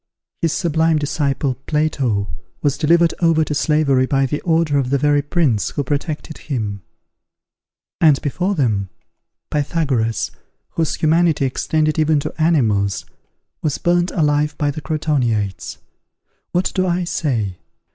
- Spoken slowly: Yes, slow, 130 wpm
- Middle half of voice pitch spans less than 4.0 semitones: Yes, average, 3.3 semitones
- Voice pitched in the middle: Yes, medium, 150 Hz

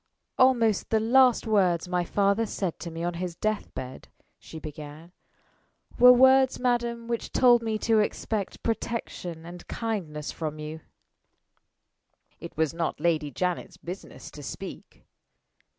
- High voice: Yes, high, 195 Hz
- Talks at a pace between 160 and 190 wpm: No, slow, 135 wpm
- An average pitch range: No, wide, 5.7 semitones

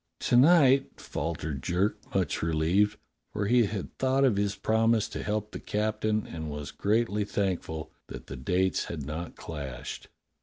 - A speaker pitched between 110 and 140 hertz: No, low, 100 Hz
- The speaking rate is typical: Yes, average, 155 wpm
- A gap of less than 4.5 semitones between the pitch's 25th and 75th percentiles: No, average, 5.3 semitones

